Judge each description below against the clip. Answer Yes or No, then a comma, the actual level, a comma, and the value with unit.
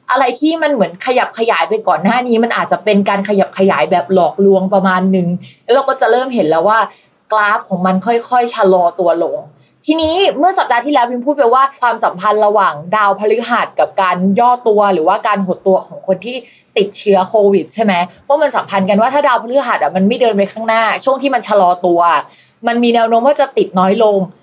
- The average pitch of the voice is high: Yes, high, 215 Hz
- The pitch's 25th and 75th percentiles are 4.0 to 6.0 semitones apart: Yes, average, 4.3 semitones